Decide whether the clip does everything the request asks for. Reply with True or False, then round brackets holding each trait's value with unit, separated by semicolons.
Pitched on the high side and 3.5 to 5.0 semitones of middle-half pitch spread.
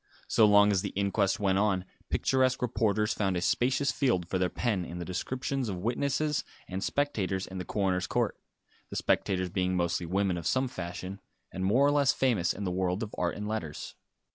False (100 Hz; 4.7 semitones)